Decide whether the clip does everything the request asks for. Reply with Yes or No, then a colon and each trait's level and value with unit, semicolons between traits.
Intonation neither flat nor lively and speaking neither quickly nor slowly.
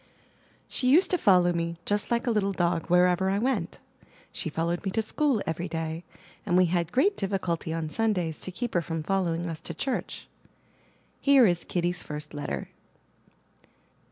Yes: average, 3.9 semitones; average, 170 wpm